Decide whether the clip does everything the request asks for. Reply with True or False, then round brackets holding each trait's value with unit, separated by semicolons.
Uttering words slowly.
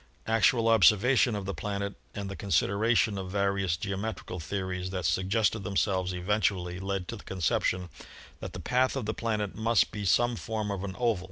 False (175 wpm)